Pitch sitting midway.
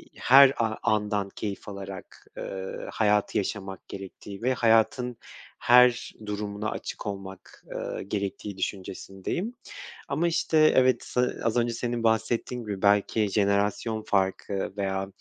No: low, 105 Hz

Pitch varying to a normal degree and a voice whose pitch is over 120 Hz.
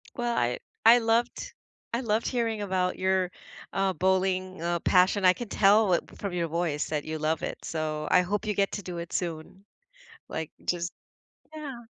Yes: average, 3.9 semitones; medium, 185 Hz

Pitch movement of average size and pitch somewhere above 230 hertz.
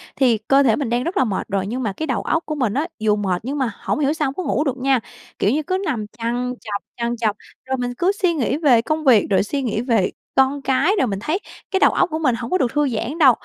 Yes: average, 4.5 semitones; very high, 255 Hz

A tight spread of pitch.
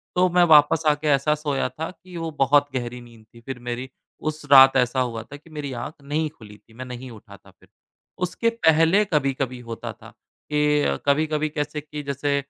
No: average, 3.3 semitones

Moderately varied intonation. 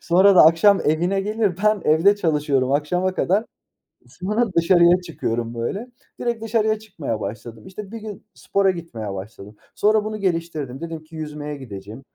No: wide, 6.2 semitones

